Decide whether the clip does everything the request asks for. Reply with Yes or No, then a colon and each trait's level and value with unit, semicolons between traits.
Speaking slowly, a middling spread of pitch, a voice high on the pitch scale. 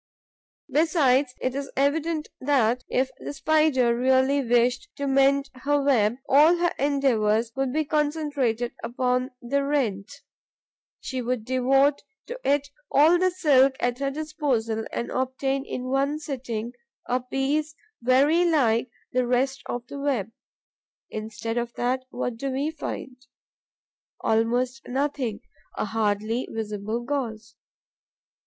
Yes: slow, 130 wpm; average, 3.0 semitones; very high, 260 Hz